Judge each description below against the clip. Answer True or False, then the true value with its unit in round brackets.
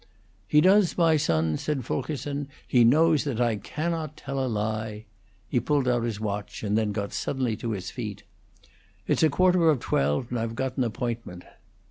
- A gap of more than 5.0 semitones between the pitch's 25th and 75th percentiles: True (5.4 semitones)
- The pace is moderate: True (175 wpm)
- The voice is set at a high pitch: False (120 Hz)